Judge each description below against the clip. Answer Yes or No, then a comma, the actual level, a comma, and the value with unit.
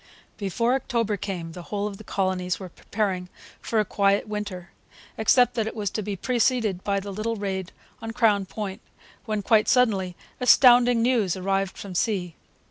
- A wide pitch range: No, average, 3.0 semitones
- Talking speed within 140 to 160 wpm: No, average, 175 wpm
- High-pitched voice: Yes, high, 205 Hz